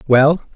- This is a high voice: No, medium, 145 Hz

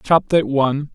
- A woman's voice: No, male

